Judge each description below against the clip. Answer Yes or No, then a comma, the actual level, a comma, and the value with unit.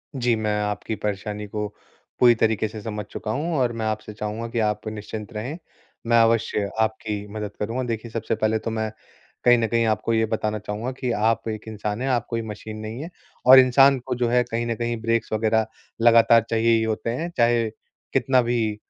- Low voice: Yes, low, 110 Hz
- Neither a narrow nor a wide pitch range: No, narrow, 1.7 semitones